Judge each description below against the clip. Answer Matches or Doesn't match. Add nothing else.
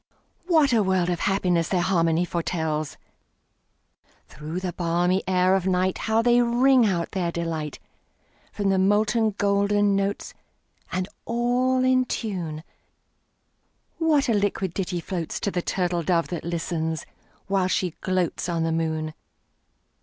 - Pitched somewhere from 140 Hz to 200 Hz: Matches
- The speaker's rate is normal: Doesn't match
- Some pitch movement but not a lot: Matches